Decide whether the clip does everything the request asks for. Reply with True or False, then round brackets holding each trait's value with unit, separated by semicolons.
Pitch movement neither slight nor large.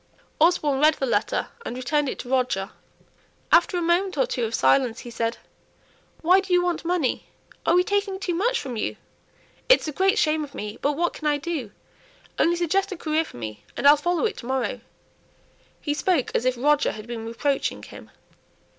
False (5.9 semitones)